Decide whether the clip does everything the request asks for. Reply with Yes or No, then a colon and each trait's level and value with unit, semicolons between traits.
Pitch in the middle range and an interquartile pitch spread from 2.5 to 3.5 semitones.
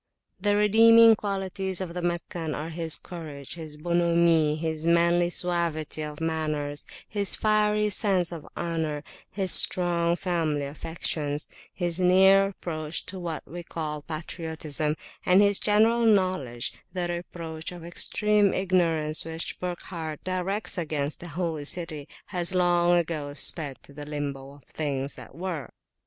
Yes: medium, 170 Hz; average, 3.0 semitones